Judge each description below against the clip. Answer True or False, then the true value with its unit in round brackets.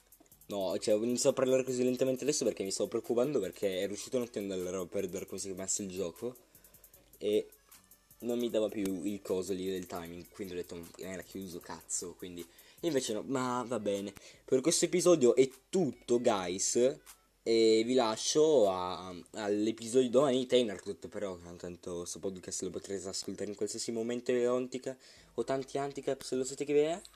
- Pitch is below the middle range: True (115 Hz)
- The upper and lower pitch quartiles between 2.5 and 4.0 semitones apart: False (5.3 semitones)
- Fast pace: True (190 wpm)